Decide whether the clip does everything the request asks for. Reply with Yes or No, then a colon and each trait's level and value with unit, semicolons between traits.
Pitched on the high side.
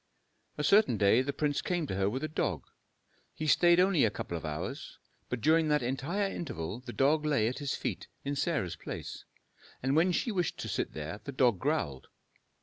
No: medium, 140 Hz